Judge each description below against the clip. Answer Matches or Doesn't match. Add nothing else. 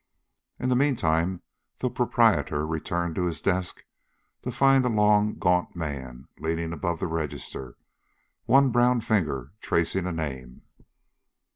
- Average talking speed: Doesn't match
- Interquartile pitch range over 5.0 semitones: Matches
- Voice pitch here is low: Matches